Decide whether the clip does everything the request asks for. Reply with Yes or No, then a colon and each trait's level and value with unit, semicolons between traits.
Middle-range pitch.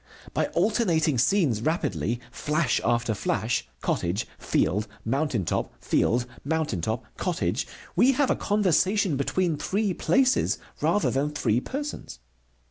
Yes: medium, 150 Hz